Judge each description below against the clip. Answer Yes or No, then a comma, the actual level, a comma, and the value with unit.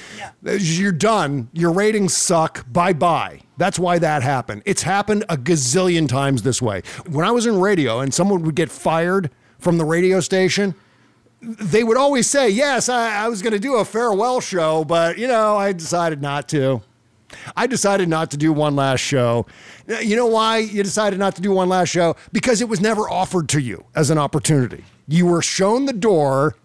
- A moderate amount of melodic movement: No, wide, 5.9 semitones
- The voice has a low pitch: No, medium, 175 Hz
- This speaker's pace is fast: No, average, 195 wpm